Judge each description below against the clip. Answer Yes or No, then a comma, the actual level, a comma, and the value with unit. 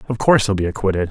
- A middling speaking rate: No, fast, 270 wpm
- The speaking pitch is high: No, low, 105 Hz